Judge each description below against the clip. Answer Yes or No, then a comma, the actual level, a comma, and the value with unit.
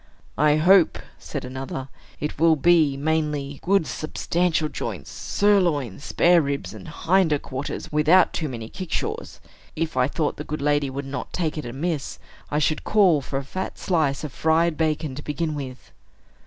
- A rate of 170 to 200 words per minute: No, average, 160 wpm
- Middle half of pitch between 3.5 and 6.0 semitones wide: No, average, 3.1 semitones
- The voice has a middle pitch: Yes, medium, 155 Hz